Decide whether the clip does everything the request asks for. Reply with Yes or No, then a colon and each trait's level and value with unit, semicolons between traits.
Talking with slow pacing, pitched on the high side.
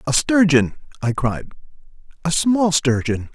No: slow, 125 wpm; medium, 155 Hz